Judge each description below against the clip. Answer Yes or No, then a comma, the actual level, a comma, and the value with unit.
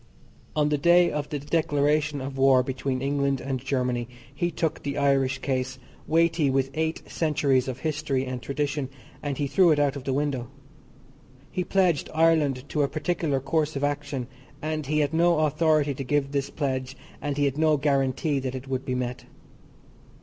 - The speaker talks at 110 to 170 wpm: No, average, 180 wpm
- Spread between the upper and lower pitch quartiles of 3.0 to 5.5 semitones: No, narrow, 2.4 semitones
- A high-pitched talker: No, medium, 140 Hz